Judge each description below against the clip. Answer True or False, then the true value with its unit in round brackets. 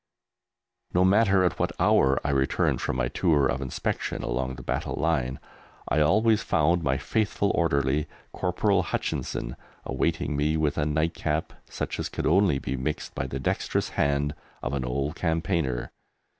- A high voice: False (75 Hz)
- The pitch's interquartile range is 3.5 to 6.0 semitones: True (3.9 semitones)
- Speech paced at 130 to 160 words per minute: True (155 wpm)